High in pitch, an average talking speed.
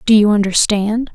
Yes: high, 215 Hz; average, 155 wpm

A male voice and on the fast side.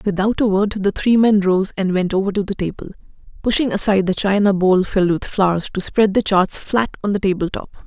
No: female; fast, 230 wpm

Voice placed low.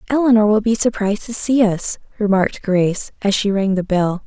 No: high, 210 Hz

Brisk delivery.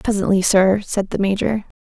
No: average, 165 wpm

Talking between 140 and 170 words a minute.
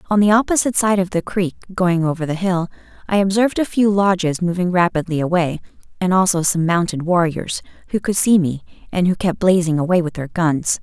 No: average, 200 wpm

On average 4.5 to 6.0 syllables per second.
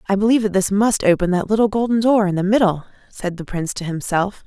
No: 6.4 syllables/s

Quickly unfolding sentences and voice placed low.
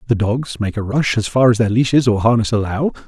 Yes: fast, 255 wpm; low, 115 Hz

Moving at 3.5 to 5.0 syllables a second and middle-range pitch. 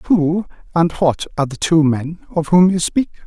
Yes: 4.6 syllables/s; medium, 165 Hz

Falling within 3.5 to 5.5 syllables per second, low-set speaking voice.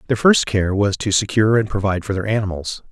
No: 6.3 syllables/s; low, 105 Hz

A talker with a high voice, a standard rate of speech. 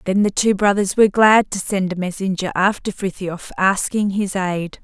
Yes: high, 195 Hz; average, 185 wpm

